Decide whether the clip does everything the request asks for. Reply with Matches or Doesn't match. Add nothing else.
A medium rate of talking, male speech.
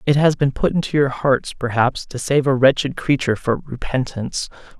Matches